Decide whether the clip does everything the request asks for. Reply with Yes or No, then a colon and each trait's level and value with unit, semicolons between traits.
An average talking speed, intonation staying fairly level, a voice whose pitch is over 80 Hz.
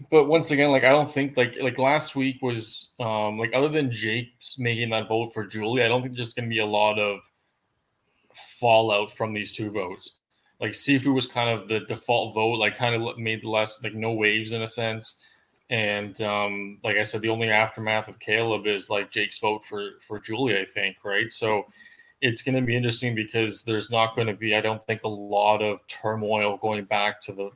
No: fast, 220 wpm; narrow, 2.3 semitones; low, 110 Hz